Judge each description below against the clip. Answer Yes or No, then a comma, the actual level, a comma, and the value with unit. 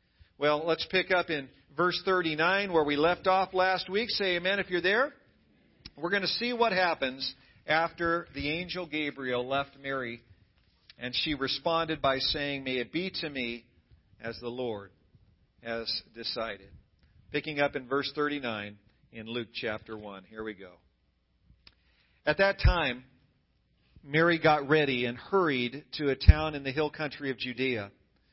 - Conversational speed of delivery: Yes, average, 155 wpm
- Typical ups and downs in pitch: No, wide, 6.1 semitones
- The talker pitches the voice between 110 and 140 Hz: Yes, low, 135 Hz